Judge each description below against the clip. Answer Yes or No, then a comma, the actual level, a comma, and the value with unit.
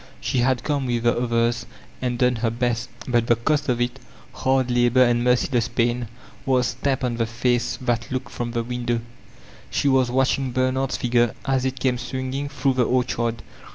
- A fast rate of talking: No, average, 185 wpm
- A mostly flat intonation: Yes, narrow, 1.5 semitones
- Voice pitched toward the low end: Yes, low, 125 Hz